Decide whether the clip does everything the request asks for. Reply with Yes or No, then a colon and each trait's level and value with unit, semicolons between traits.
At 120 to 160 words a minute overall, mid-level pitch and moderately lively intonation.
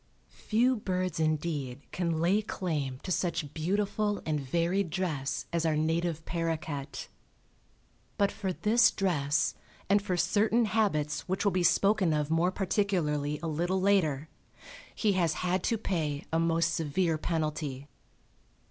Yes: average, 140 wpm; medium, 170 Hz; average, 3.9 semitones